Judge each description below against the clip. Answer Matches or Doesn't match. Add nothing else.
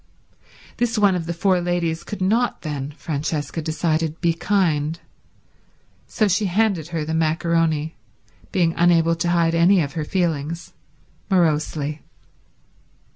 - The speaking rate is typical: Doesn't match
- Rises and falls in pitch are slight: Matches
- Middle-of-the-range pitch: Matches